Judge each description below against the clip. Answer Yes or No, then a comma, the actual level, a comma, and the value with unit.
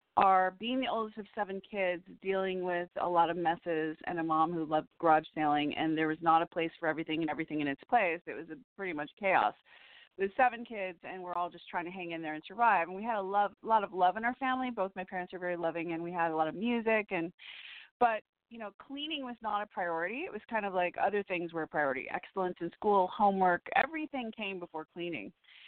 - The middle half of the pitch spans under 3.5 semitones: No, average, 4.4 semitones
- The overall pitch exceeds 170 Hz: Yes, medium, 185 Hz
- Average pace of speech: No, fast, 245 wpm